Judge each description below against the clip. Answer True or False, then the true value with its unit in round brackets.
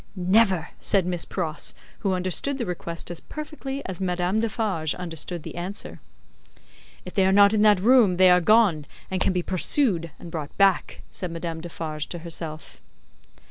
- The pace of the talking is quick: False (170 wpm)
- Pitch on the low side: False (180 Hz)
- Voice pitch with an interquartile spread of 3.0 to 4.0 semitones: True (3.4 semitones)